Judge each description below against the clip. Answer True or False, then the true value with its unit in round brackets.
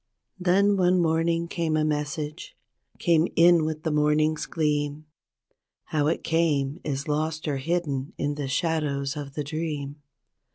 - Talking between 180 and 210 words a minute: False (140 wpm)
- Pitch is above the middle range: False (155 Hz)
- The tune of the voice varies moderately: False (2.2 semitones)